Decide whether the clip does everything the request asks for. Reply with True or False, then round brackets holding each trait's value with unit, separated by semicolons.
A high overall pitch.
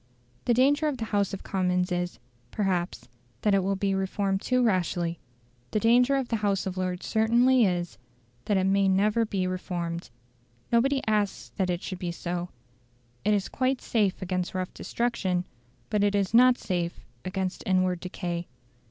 True (195 Hz)